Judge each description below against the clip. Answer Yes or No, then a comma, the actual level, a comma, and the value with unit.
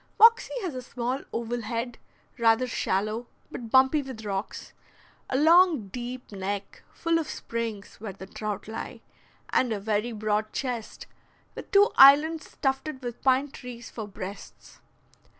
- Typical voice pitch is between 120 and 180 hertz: No, high, 240 Hz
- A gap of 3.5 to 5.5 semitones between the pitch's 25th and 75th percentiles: Yes, average, 3.8 semitones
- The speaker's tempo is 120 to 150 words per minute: Yes, average, 145 wpm